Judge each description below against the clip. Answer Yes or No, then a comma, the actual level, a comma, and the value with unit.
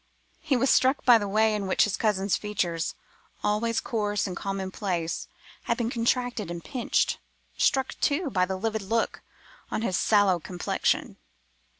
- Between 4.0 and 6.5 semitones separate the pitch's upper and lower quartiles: No, average, 3.6 semitones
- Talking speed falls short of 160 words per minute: Yes, average, 150 wpm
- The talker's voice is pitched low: No, high, 210 Hz